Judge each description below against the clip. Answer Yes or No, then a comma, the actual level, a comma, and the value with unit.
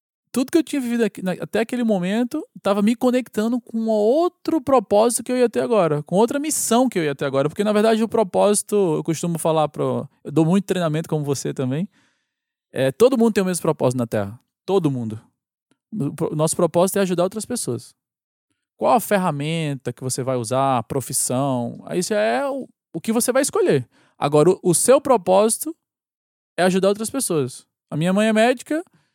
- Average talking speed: No, fast, 190 wpm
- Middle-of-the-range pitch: No, high, 200 Hz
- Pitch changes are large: Yes, wide, 7.5 semitones